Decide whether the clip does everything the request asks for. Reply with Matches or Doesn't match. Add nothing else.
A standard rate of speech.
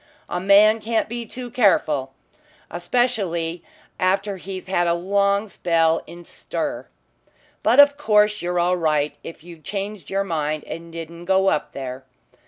Matches